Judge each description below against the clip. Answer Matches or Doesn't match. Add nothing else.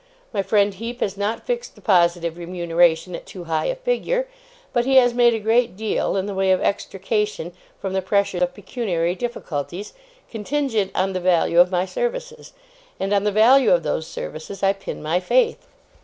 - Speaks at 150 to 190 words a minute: Matches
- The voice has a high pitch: Matches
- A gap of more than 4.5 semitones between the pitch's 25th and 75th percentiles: Matches